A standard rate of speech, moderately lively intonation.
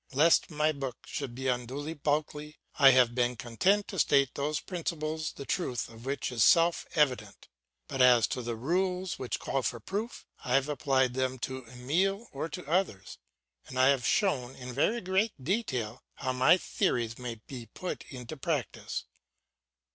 Yes: average, 170 wpm; average, 4.5 semitones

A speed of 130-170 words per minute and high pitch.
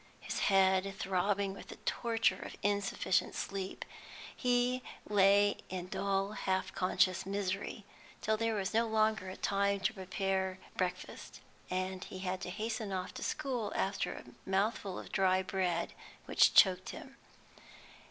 Yes: average, 140 wpm; high, 195 Hz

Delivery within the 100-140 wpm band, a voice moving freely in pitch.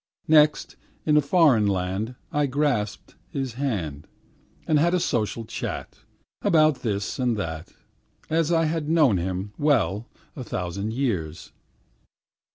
Yes: slow, 135 wpm; wide, 7.1 semitones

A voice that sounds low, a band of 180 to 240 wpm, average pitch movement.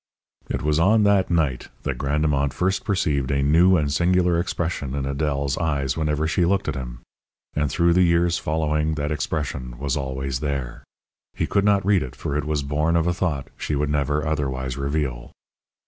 Yes: very low, 75 Hz; average, 185 wpm; average, 3.6 semitones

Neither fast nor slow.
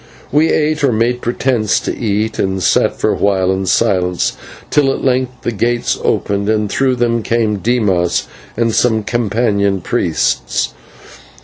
Yes: average, 150 wpm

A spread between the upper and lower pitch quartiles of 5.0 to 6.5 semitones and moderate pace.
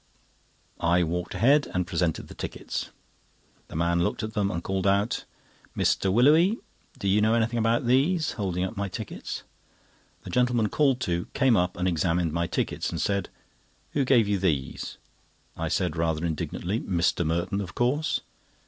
Yes: wide, 5.4 semitones; average, 165 wpm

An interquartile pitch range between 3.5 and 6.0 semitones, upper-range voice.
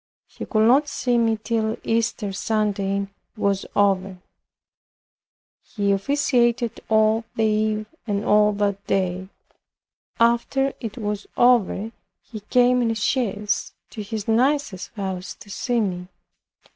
No: average, 2.8 semitones; high, 215 Hz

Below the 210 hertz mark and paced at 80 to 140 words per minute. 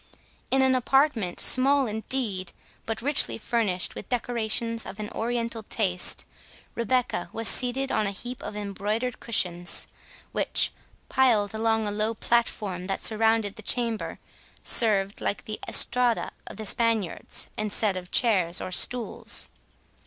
No: high, 220 Hz; slow, 135 wpm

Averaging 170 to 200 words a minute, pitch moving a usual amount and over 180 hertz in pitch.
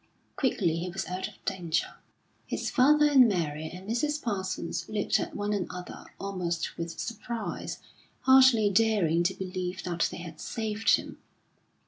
No: average, 145 wpm; average, 4.5 semitones; high, 190 Hz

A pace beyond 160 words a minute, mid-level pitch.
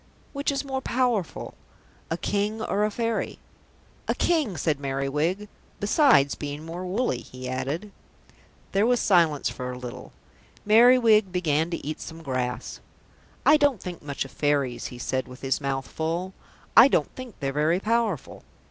No: average, 155 wpm; medium, 175 Hz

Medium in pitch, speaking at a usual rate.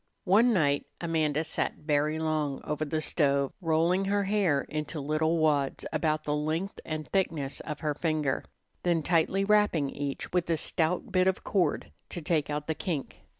Yes: medium, 155 Hz; average, 170 wpm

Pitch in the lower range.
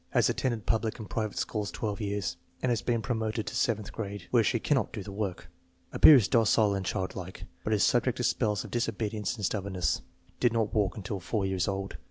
Yes: low, 105 Hz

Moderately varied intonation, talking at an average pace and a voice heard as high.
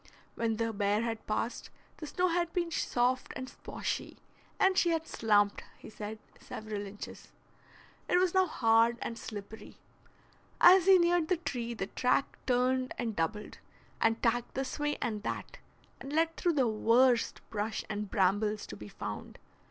No: wide, 6.5 semitones; average, 160 wpm; high, 235 Hz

